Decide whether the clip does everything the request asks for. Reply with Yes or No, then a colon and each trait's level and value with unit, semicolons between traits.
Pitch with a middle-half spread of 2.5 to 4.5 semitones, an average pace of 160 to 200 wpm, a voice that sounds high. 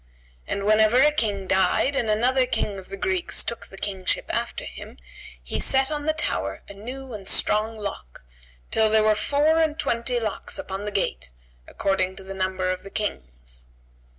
No: average, 4.9 semitones; average, 180 wpm; high, 210 Hz